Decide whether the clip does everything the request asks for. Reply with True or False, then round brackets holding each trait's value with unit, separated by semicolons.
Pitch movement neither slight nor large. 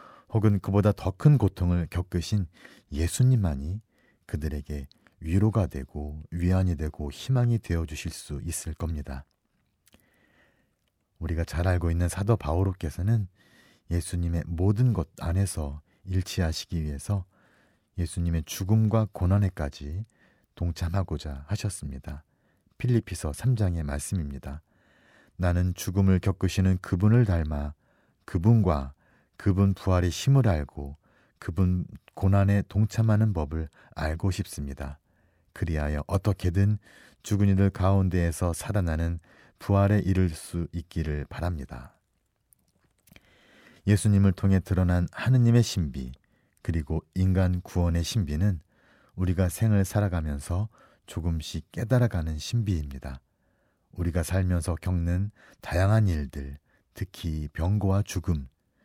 True (3.7 semitones)